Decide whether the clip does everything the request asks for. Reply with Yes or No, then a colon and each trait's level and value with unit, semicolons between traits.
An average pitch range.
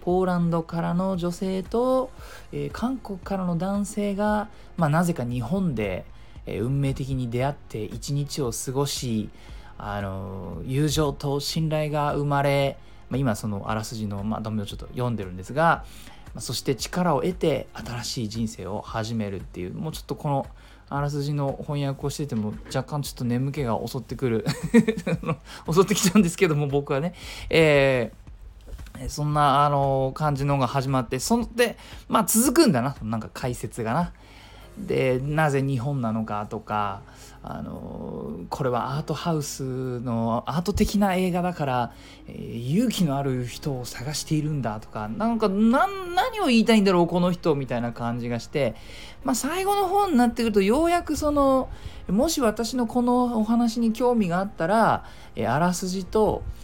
No: wide, 8.0 semitones